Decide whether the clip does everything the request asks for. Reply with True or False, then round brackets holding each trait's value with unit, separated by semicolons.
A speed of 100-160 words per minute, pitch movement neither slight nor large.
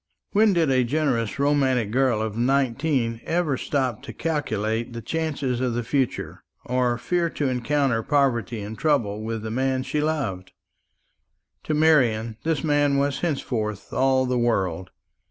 True (150 wpm; 4.1 semitones)